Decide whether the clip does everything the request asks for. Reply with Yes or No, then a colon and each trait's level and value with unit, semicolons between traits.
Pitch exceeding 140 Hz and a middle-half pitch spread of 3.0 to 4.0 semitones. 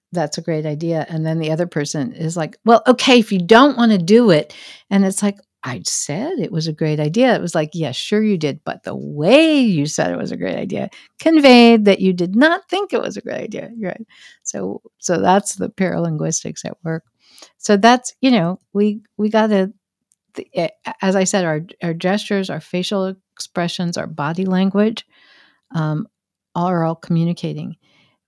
No: high, 190 Hz; average, 5.2 semitones